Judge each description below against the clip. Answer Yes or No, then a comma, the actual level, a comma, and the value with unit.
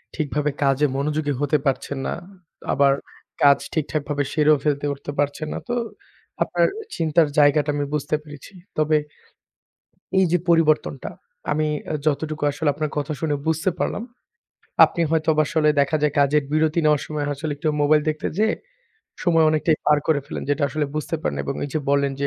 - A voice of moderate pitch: Yes, medium, 150 Hz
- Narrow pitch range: Yes, narrow, 1.4 semitones